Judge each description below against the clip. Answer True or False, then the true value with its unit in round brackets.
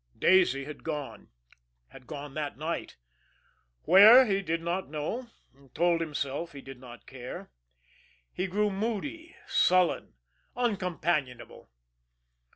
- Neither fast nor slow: False (115 wpm)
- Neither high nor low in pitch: True (165 Hz)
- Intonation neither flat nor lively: False (5.7 semitones)